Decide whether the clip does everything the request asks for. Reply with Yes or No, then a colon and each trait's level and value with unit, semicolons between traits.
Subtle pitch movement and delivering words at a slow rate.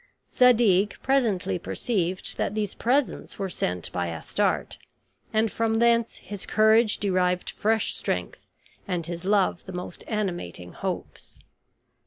No: average, 3.9 semitones; slow, 125 wpm